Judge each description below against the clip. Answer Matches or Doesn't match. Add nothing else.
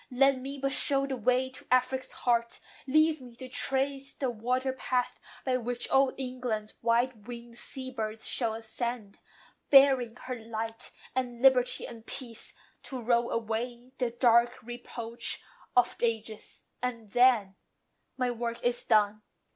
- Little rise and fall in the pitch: Matches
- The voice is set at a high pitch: Matches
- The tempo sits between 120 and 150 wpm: Matches